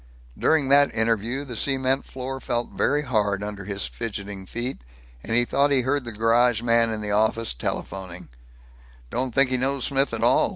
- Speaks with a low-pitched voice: Yes, low, 120 Hz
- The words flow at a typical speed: Yes, average, 180 wpm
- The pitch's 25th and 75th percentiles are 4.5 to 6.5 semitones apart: No, average, 3.7 semitones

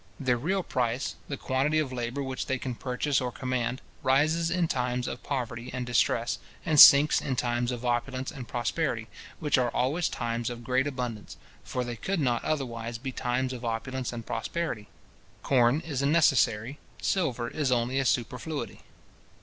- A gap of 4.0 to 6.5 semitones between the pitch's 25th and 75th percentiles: No, average, 2.8 semitones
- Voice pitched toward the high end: No, low, 125 Hz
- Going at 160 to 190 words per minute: Yes, average, 170 wpm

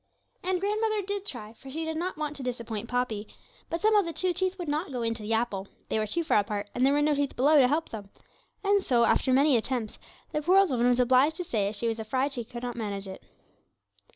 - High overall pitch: Yes, very high, 260 Hz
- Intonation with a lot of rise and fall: Yes, wide, 6.3 semitones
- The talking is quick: Yes, fast, 245 wpm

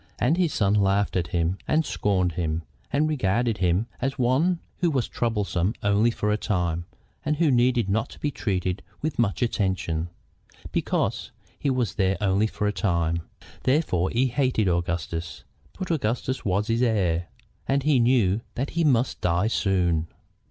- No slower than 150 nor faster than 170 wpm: Yes, average, 160 wpm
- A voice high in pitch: No, low, 105 Hz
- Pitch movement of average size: No, wide, 6.0 semitones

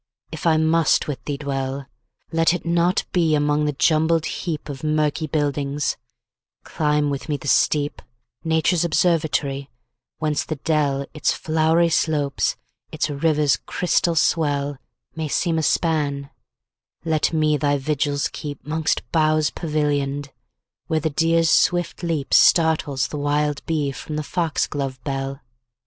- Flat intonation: Yes, narrow, 2.1 semitones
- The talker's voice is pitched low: No, medium, 150 Hz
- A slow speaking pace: Yes, slow, 120 wpm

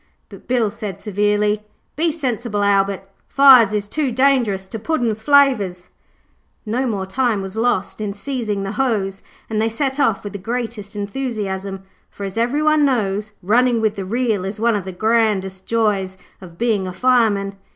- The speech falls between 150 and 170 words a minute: Yes, average, 165 wpm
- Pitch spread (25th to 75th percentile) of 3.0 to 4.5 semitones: Yes, average, 3.8 semitones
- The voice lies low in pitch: No, high, 215 Hz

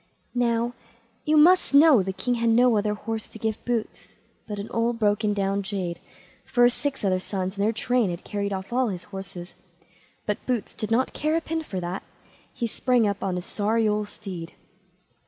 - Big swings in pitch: No, average, 3.7 semitones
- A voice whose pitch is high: Yes, high, 215 Hz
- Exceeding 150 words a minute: Yes, average, 195 wpm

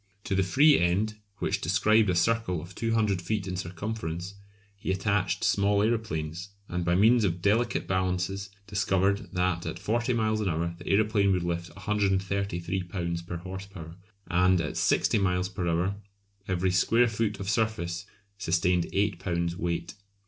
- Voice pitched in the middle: No, very low, 95 Hz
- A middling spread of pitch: Yes, average, 3.2 semitones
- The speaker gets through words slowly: No, average, 160 wpm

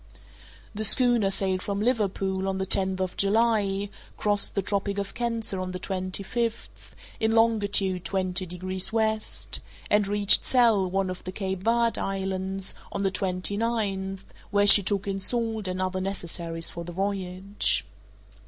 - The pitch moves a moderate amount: No, narrow, 2.2 semitones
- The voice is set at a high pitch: Yes, high, 195 Hz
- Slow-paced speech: No, average, 155 wpm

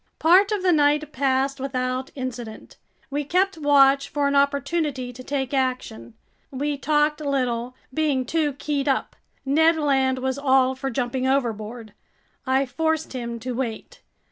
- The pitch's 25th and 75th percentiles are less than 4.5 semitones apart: Yes, narrow, 2.5 semitones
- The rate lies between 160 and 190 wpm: No, average, 145 wpm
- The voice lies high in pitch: Yes, very high, 275 Hz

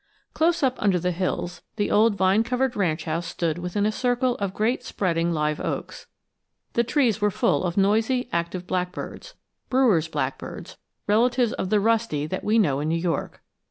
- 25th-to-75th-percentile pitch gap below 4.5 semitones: No, average, 5.2 semitones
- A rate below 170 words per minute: No, average, 175 wpm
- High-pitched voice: Yes, high, 200 Hz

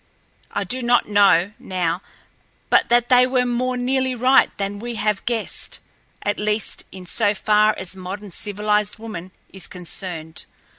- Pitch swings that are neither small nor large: Yes, average, 4.0 semitones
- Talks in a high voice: Yes, high, 210 Hz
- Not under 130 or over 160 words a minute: Yes, average, 150 wpm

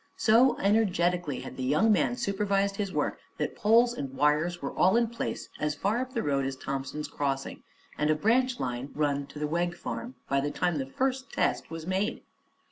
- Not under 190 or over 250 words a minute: Yes, average, 200 wpm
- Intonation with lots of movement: Yes, wide, 7.2 semitones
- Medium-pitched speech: Yes, medium, 175 Hz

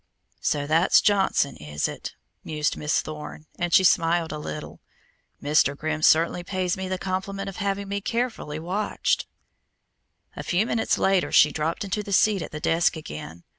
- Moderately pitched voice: Yes, medium, 175 Hz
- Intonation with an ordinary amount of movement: Yes, average, 4.2 semitones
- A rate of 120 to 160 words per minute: No, average, 170 wpm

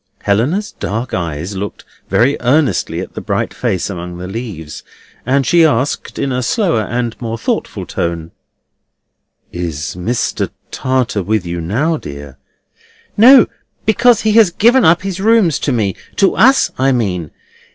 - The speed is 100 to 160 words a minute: Yes, average, 145 wpm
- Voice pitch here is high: No, low, 120 Hz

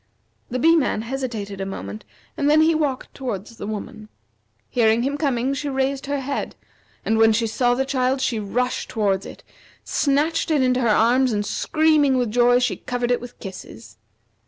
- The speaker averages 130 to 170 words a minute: No, average, 180 wpm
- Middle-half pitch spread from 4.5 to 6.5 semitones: No, average, 3.8 semitones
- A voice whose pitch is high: Yes, very high, 250 Hz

